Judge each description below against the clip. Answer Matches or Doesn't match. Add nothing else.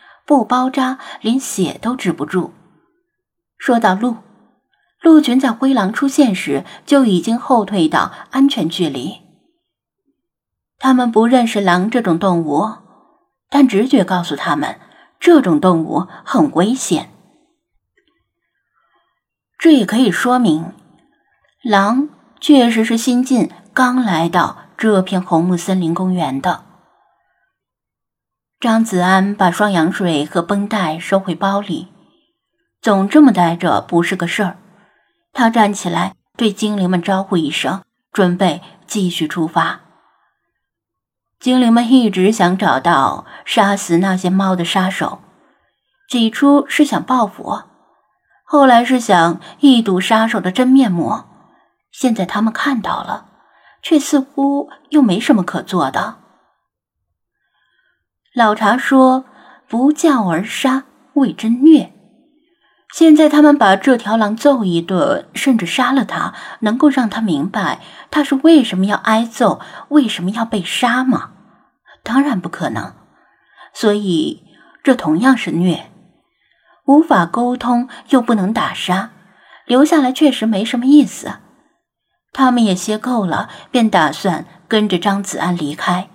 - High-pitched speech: Matches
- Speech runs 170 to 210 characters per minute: Matches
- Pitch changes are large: Matches